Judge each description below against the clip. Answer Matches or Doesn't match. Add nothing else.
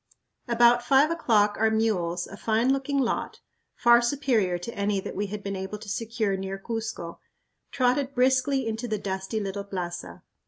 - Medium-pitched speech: Doesn't match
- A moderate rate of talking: Matches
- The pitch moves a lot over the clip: Doesn't match